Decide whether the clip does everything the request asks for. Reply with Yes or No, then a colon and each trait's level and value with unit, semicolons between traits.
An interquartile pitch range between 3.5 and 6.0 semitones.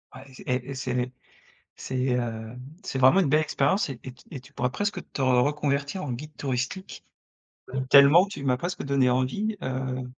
No: average, 2.8 semitones